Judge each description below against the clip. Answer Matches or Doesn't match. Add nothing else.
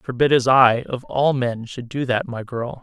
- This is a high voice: Doesn't match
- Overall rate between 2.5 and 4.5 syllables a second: Matches